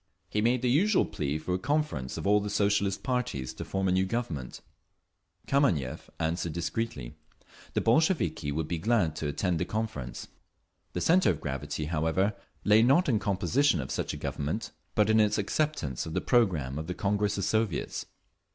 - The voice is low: Yes, low, 100 Hz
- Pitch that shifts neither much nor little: No, wide, 6.6 semitones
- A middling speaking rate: Yes, average, 180 wpm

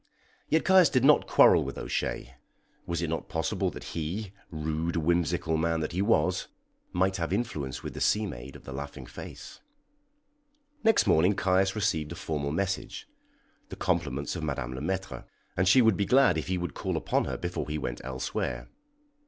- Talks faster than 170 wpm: Yes, average, 180 wpm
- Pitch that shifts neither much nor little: Yes, average, 4.0 semitones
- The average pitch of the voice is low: Yes, very low, 85 Hz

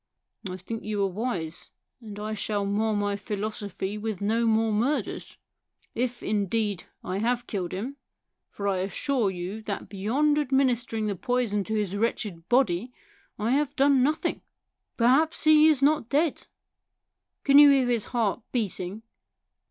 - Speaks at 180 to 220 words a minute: No, average, 155 wpm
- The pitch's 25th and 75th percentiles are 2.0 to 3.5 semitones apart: No, average, 4.0 semitones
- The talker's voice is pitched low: No, high, 220 Hz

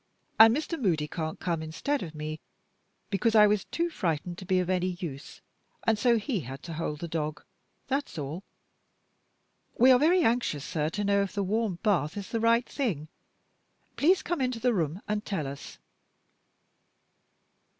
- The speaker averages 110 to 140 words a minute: No, average, 170 wpm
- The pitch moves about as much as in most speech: No, wide, 6.6 semitones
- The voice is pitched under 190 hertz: No, high, 195 Hz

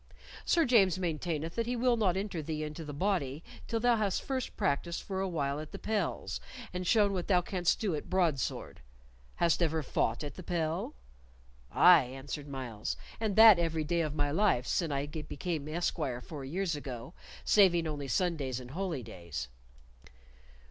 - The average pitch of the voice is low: No, medium, 165 Hz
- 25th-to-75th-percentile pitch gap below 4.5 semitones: No, average, 4.8 semitones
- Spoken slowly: No, average, 175 wpm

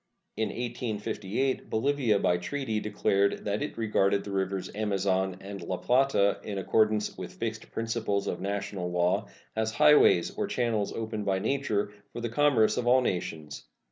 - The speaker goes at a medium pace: Yes, average, 155 wpm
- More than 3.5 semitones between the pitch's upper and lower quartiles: No, average, 3.1 semitones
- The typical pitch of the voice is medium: No, low, 105 Hz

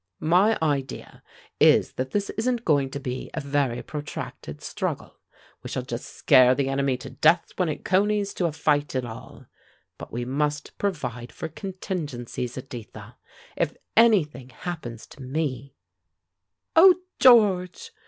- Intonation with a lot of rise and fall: Yes, wide, 6.3 semitones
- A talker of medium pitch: Yes, medium, 145 Hz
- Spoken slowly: No, average, 145 wpm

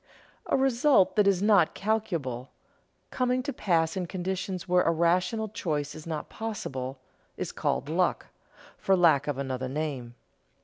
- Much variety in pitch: Yes, wide, 6.0 semitones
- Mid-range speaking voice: Yes, medium, 175 Hz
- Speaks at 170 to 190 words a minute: No, average, 145 wpm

